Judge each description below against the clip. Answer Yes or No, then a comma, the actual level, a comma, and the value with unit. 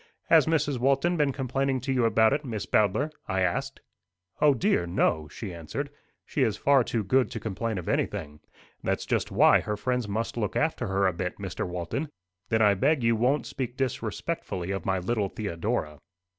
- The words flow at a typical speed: Yes, average, 185 wpm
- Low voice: Yes, low, 115 Hz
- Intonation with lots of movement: Yes, wide, 5.9 semitones